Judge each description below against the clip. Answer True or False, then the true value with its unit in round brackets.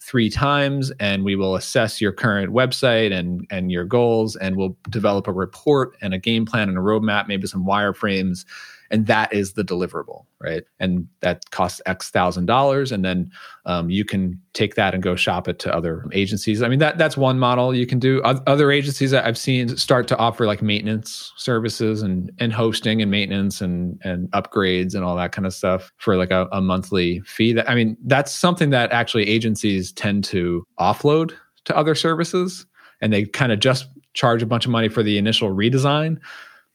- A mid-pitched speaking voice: False (110 Hz)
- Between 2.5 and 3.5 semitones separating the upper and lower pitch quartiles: False (4.9 semitones)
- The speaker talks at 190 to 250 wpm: True (200 wpm)